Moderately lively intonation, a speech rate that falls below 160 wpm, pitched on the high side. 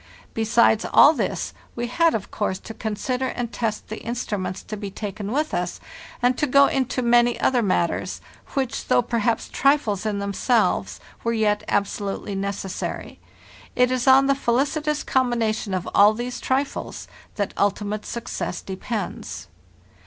Yes: average, 3.7 semitones; average, 150 wpm; high, 230 Hz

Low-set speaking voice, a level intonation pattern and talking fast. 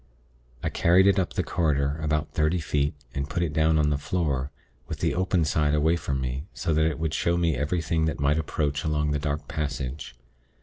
Yes: very low, 75 Hz; narrow, 2.1 semitones; fast, 210 wpm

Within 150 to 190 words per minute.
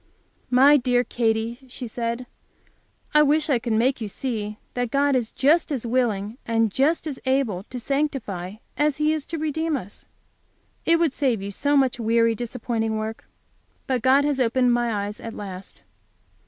Yes: average, 170 wpm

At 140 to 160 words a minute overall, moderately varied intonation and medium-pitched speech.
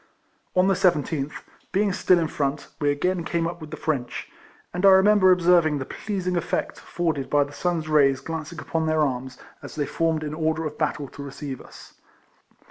No: average, 190 wpm; average, 3.4 semitones; medium, 160 Hz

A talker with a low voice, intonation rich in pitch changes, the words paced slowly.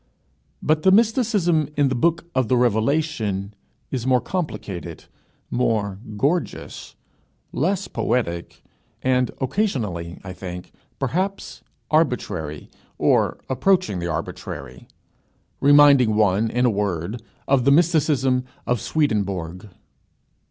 Yes: low, 125 Hz; wide, 7.6 semitones; slow, 105 wpm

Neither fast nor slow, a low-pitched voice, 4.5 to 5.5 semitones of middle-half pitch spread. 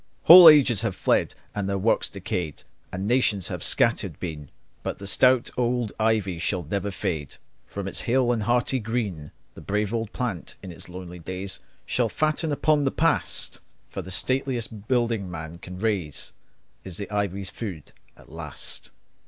Yes: average, 165 wpm; low, 100 Hz; average, 4.8 semitones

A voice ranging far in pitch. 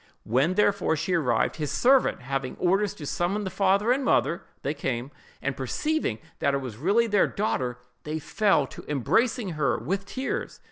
Yes: wide, 7.1 semitones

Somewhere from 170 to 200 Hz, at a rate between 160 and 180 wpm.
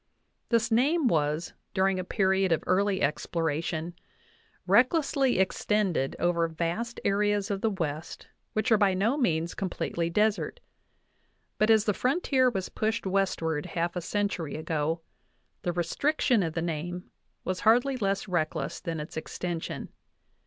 No: high, 190 Hz; average, 140 wpm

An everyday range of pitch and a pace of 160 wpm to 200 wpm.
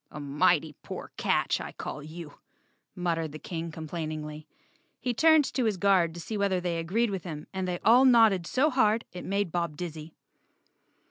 Yes: average, 4.7 semitones; average, 180 wpm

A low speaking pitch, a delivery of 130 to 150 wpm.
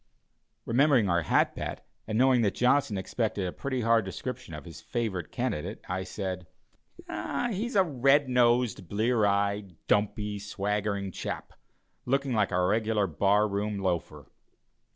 Yes: low, 105 Hz; average, 145 wpm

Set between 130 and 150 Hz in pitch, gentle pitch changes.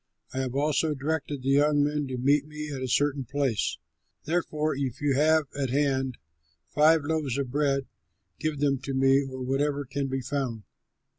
Yes: medium, 140 Hz; narrow, 1.9 semitones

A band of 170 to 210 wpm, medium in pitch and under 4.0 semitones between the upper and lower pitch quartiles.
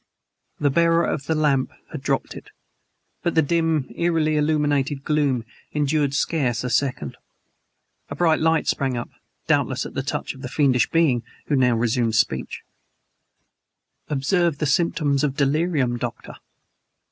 No: average, 145 wpm; medium, 145 Hz; average, 3.4 semitones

